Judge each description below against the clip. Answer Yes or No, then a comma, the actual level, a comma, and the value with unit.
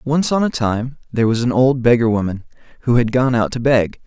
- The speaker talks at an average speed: No, fast, 235 wpm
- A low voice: Yes, low, 120 Hz